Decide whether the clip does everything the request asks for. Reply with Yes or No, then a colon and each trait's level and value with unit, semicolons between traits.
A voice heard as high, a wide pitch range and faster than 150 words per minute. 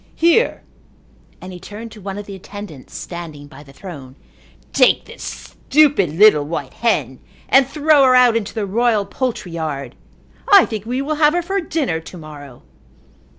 Yes: high, 205 Hz; wide, 8.4 semitones; average, 170 wpm